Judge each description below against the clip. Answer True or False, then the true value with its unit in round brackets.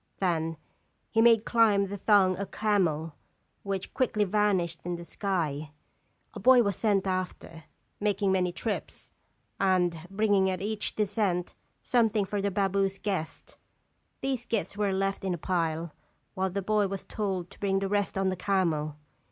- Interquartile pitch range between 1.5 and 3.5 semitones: True (2.5 semitones)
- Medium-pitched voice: False (195 Hz)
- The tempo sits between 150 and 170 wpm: True (160 wpm)